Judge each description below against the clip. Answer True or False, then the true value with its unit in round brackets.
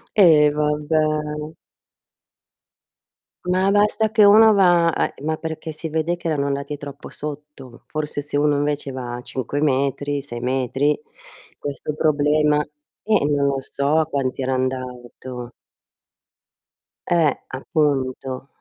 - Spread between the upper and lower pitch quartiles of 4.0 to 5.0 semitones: False (2.7 semitones)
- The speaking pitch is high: False (150 Hz)